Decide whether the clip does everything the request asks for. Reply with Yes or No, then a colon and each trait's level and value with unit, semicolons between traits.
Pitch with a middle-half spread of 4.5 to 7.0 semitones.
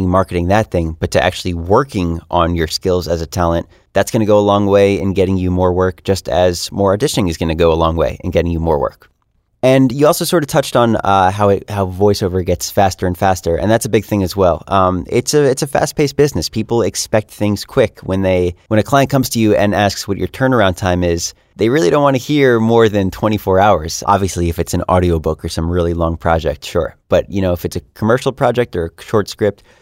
No: average, 3.4 semitones